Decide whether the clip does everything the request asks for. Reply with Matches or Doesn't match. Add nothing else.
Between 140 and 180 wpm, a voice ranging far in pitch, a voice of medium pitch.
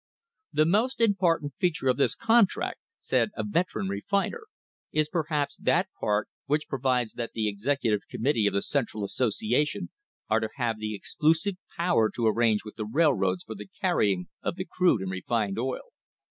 Doesn't match